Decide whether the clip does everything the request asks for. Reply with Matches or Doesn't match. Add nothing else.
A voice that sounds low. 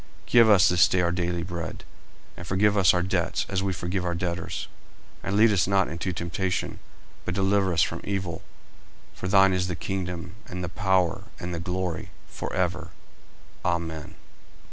Matches